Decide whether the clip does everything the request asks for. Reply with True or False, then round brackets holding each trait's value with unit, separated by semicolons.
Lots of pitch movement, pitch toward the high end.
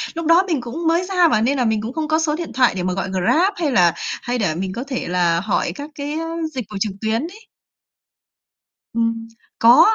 True (7.2 semitones; 245 Hz)